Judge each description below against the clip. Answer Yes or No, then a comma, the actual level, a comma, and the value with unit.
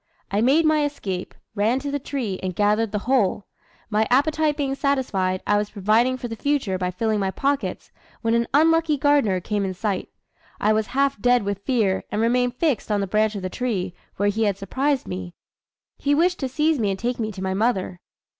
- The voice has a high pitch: Yes, high, 225 Hz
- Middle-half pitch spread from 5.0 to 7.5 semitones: Yes, wide, 5.5 semitones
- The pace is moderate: No, fast, 210 wpm